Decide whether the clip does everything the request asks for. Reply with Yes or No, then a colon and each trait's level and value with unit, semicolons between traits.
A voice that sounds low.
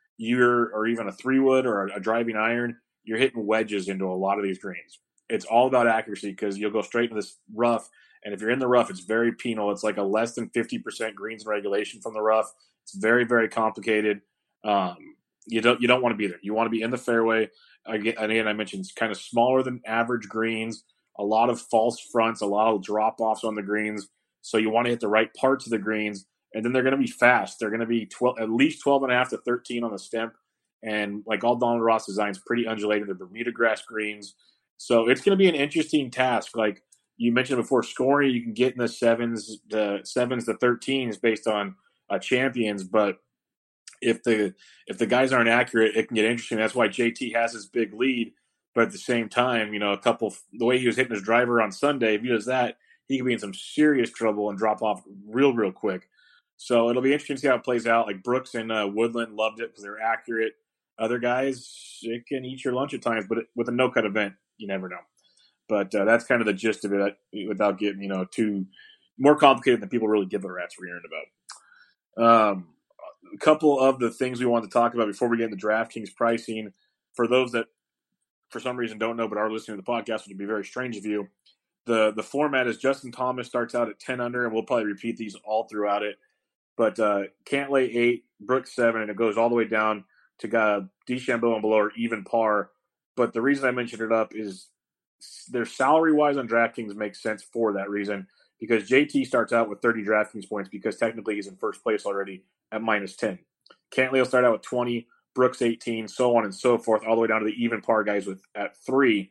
Yes: low, 115 Hz